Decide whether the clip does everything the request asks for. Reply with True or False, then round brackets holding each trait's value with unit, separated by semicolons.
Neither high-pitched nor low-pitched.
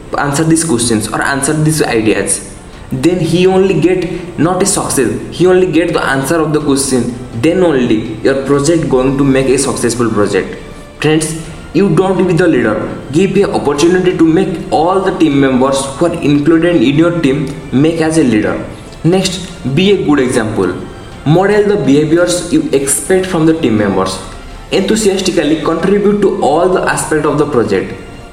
True (155 Hz)